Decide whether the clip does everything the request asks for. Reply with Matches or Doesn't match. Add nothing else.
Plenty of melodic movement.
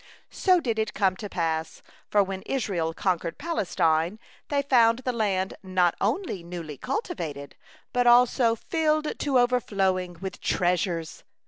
Matches